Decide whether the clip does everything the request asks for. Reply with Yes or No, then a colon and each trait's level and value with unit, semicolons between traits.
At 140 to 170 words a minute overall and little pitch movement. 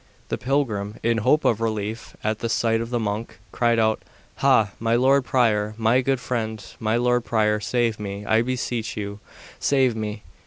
No: average, 180 wpm; narrow, 2.2 semitones